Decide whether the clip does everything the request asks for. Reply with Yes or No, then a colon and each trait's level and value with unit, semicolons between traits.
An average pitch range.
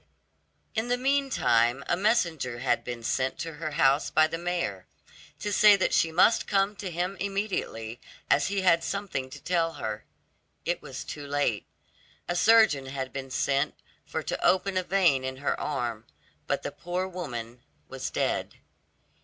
No: wide, 6.5 semitones